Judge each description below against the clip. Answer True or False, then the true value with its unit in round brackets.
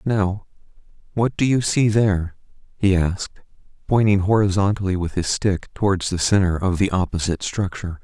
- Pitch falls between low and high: False (95 Hz)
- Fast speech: False (150 wpm)